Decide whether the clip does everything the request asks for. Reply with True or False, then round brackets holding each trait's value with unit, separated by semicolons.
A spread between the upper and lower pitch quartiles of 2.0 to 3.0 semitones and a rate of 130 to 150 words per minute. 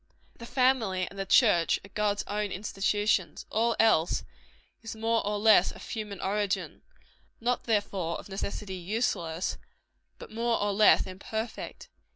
True (2.6 semitones; 145 wpm)